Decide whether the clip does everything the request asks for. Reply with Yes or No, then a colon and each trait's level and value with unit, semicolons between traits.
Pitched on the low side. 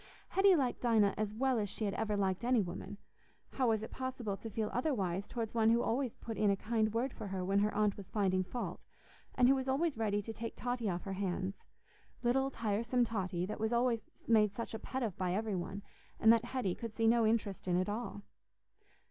No: high, 220 Hz